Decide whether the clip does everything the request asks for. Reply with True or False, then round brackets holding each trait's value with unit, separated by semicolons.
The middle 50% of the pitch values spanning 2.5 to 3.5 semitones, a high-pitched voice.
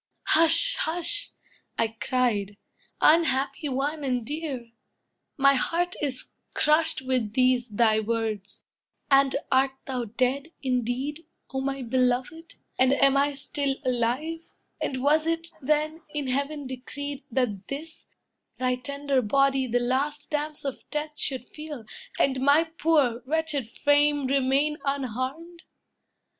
True (3.0 semitones; 275 Hz)